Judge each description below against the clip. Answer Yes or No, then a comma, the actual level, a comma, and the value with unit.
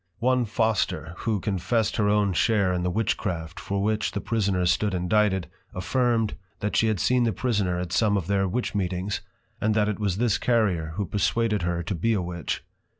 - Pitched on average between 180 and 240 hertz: No, low, 100 Hz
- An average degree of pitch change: Yes, average, 3.4 semitones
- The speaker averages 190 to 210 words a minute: Yes, average, 195 wpm